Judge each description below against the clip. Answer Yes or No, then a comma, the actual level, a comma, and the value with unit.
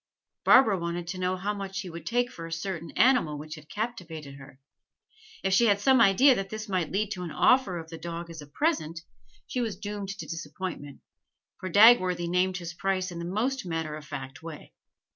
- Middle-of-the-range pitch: Yes, medium, 180 Hz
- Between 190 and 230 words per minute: Yes, fast, 205 wpm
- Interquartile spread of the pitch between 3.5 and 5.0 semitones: Yes, average, 4.0 semitones